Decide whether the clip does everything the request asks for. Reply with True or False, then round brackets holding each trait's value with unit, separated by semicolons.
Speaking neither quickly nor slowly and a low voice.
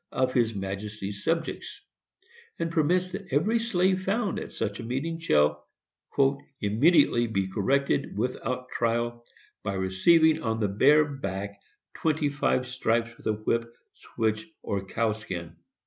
False (130 wpm; 120 Hz)